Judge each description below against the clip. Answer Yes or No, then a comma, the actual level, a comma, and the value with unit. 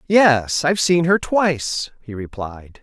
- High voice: No, medium, 145 Hz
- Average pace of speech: Yes, average, 150 wpm